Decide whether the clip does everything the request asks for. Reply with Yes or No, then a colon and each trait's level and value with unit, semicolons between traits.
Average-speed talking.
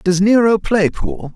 Yes: average, 175 wpm